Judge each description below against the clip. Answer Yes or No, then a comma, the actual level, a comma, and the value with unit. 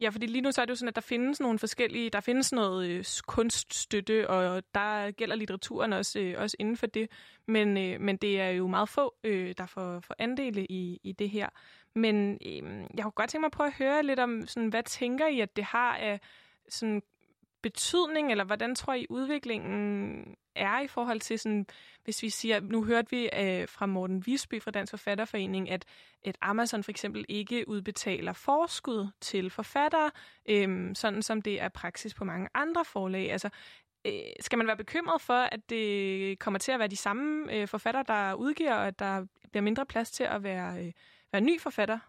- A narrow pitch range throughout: No, average, 3.3 semitones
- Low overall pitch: No, high, 215 Hz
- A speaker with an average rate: Yes, average, 205 wpm